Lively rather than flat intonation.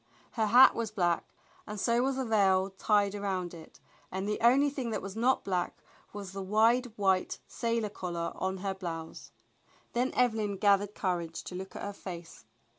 No: average, 3.3 semitones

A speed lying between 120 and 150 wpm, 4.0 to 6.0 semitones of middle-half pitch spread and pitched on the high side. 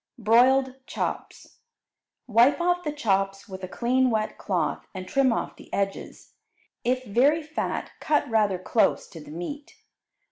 Yes: average, 145 wpm; wide, 5.5 semitones; high, 235 Hz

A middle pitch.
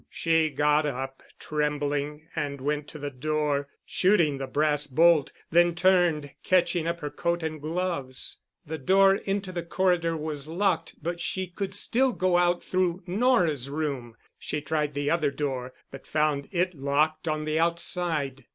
Yes: medium, 155 Hz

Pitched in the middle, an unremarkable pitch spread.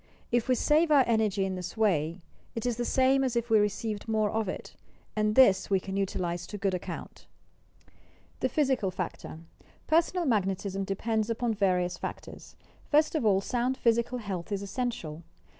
No: high, 215 Hz; average, 4.2 semitones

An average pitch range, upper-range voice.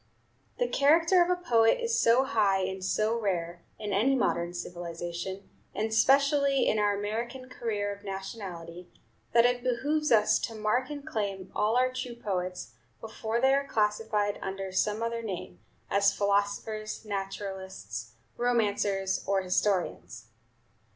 Yes: average, 4.0 semitones; high, 210 Hz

